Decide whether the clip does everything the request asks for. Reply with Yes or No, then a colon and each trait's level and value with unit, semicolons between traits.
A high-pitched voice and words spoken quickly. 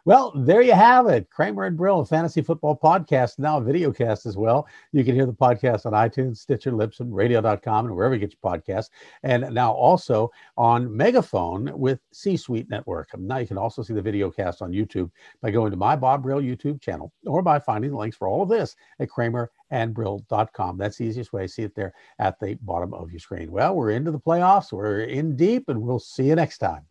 No: low, 120 Hz; fast, 225 wpm